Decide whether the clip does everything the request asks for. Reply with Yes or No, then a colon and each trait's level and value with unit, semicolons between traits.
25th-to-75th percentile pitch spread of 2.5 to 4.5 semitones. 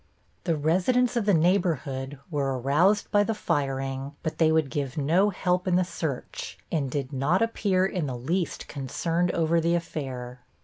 No: average, 5.0 semitones